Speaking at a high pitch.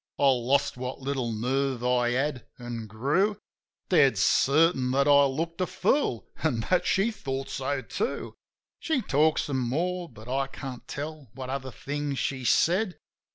No: low, 135 Hz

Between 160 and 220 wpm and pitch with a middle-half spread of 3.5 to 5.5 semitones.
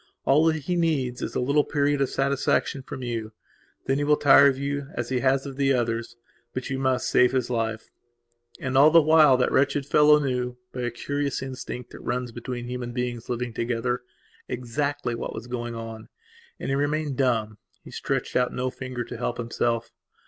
No: average, 190 wpm; narrow, 2.6 semitones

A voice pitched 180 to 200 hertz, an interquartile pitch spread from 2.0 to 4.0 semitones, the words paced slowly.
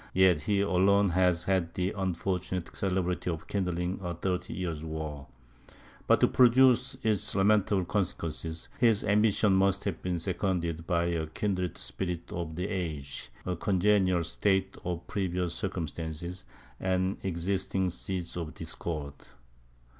No: very low, 90 Hz; narrow, 2.5 semitones; slow, 130 wpm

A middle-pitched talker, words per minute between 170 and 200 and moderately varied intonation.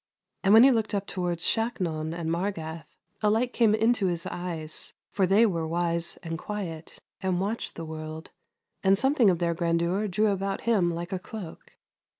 Yes: medium, 180 Hz; average, 175 wpm; average, 4.0 semitones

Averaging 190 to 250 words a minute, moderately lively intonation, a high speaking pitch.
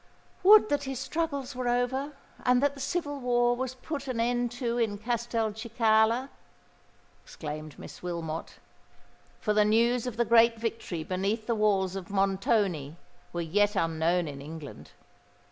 No: average, 145 wpm; average, 4.5 semitones; high, 230 Hz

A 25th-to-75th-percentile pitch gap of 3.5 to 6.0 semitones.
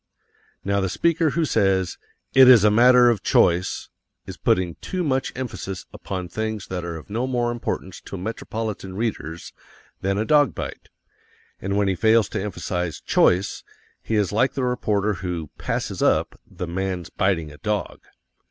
Yes: average, 4.4 semitones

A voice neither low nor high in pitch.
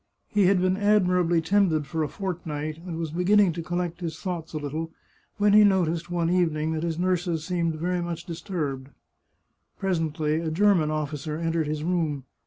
Yes: medium, 170 Hz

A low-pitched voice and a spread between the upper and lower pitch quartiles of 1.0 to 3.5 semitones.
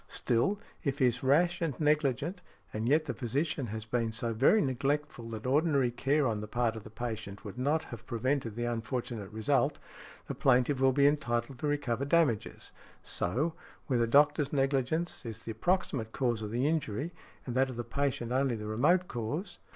No: low, 130 Hz; average, 4.1 semitones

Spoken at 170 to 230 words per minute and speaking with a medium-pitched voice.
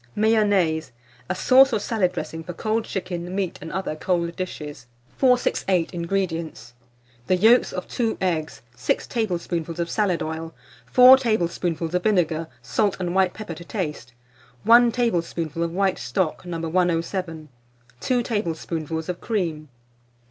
No: average, 140 wpm; medium, 180 Hz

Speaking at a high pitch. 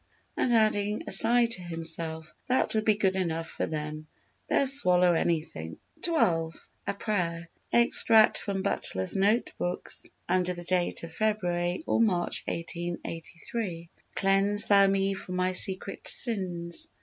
No: medium, 180 Hz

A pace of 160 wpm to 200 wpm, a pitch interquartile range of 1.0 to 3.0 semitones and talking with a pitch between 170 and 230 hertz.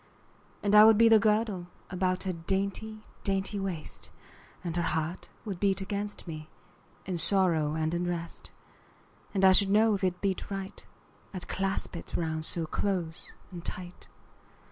Yes: average, 165 wpm; average, 2.7 semitones; high, 190 Hz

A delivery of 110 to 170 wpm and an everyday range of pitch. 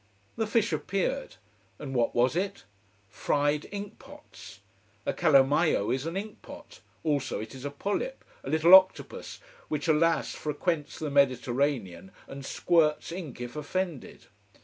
No: average, 140 wpm; wide, 5.7 semitones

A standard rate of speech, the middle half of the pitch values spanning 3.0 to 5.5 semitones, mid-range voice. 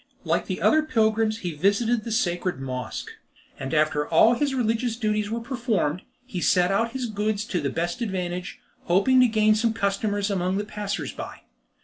No: average, 175 wpm; average, 4.2 semitones; high, 210 Hz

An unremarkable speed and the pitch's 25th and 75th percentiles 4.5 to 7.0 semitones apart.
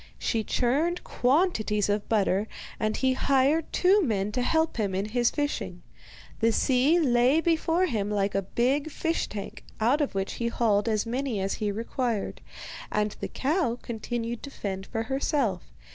Yes: average, 165 wpm; average, 5.2 semitones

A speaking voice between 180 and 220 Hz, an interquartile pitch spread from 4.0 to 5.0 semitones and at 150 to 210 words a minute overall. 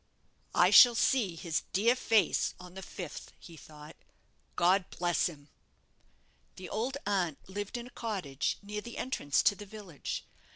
Yes: high, 190 Hz; average, 4.5 semitones; average, 155 wpm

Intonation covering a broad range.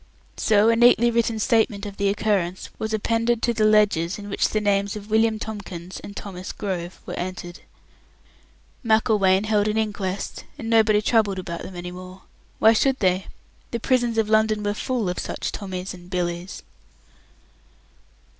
No: average, 2.9 semitones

